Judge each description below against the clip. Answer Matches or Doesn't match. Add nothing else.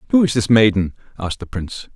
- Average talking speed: Doesn't match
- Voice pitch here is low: Matches